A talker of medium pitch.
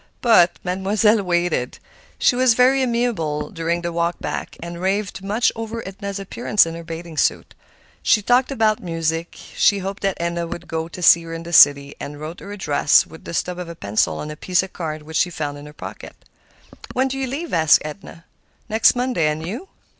Yes: medium, 175 Hz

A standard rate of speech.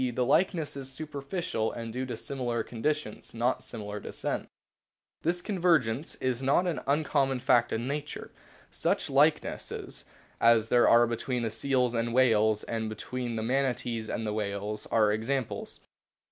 Yes: average, 150 wpm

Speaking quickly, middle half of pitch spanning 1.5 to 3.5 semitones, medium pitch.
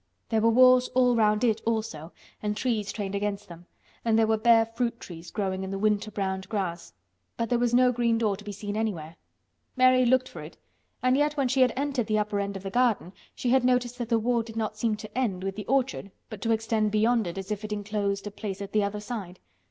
No: fast, 240 wpm; average, 3.2 semitones; high, 215 Hz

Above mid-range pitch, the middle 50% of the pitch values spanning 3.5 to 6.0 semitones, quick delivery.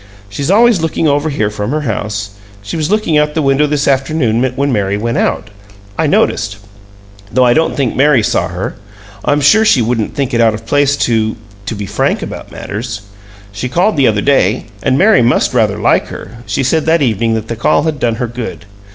No: low, 125 Hz; average, 5.2 semitones; fast, 210 wpm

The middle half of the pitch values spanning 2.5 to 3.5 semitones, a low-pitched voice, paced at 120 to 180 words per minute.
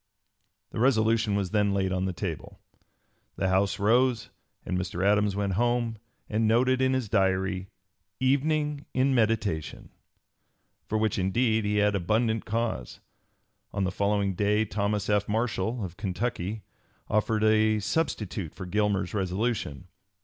Yes: average, 3.0 semitones; low, 105 Hz; average, 140 wpm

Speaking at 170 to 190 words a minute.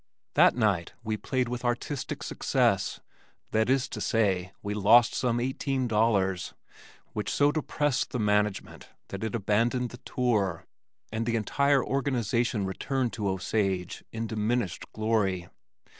No: slow, 135 wpm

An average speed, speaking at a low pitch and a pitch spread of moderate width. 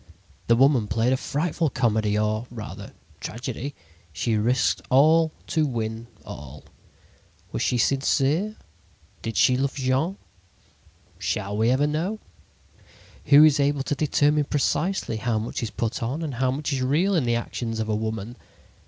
Yes: average, 155 wpm; low, 130 Hz; average, 4.5 semitones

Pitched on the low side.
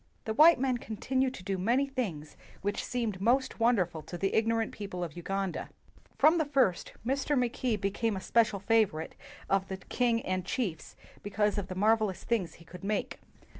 No: high, 215 Hz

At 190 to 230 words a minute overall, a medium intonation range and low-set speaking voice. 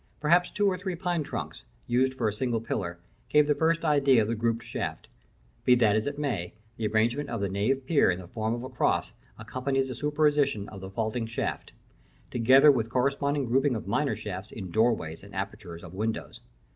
Yes: average, 200 wpm; average, 4.9 semitones; low, 120 Hz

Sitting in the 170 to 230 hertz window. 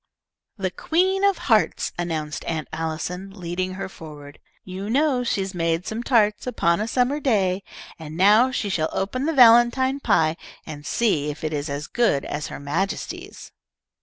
Yes: high, 190 Hz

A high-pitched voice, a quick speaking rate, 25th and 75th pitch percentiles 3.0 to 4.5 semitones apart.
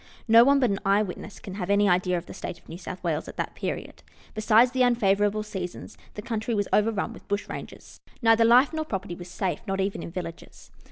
Yes: high, 205 Hz; fast, 225 wpm; average, 3.6 semitones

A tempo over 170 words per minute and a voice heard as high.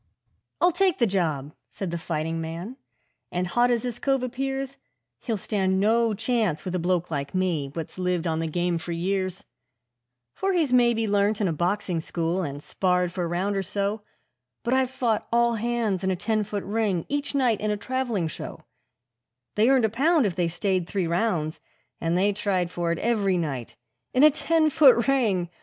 Yes: average, 190 wpm; high, 200 Hz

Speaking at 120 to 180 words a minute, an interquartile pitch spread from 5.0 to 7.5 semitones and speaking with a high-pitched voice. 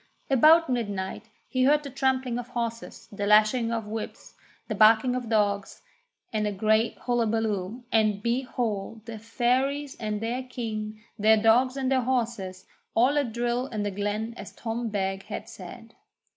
No: average, 160 wpm; average, 2.8 semitones; high, 230 Hz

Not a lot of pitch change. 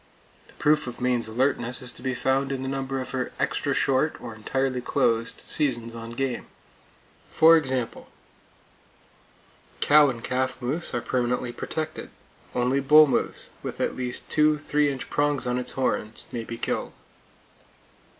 Yes: narrow, 2.2 semitones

